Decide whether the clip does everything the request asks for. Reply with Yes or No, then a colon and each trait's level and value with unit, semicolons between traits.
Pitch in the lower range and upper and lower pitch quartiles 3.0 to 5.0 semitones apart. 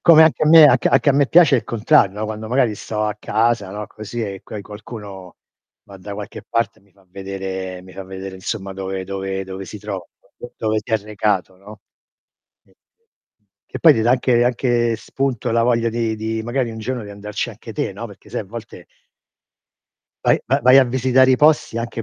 Yes: low, 110 Hz; average, 3.6 semitones